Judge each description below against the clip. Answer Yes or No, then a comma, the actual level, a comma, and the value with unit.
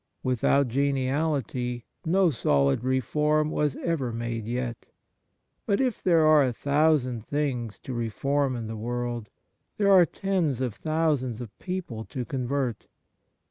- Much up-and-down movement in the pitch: No, average, 4.3 semitones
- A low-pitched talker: Yes, low, 130 Hz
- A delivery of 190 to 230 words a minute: No, average, 140 wpm